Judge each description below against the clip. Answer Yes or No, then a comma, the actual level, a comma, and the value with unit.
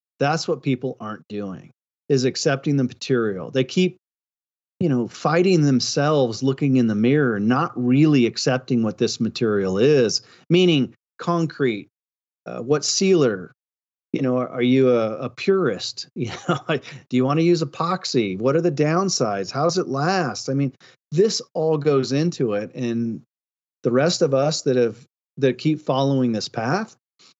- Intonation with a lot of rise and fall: No, average, 5.0 semitones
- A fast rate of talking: No, average, 160 wpm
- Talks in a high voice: No, low, 135 Hz